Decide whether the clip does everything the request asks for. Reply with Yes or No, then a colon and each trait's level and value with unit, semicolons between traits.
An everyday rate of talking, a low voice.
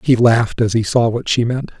No: fast, 265 wpm; low, 120 Hz